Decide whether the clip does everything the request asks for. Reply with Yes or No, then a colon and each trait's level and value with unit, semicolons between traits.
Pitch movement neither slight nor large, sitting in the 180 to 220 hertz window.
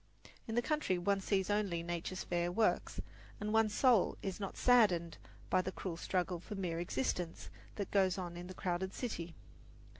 Yes: average, 3.0 semitones; medium, 185 Hz